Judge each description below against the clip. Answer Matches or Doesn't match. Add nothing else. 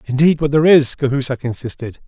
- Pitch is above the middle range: Doesn't match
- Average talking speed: Matches